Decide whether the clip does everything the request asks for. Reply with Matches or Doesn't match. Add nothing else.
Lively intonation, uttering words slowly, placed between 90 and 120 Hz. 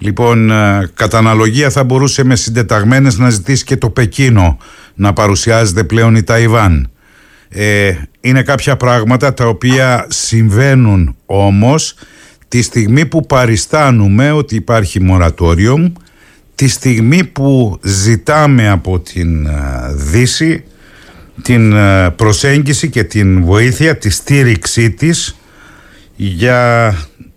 Doesn't match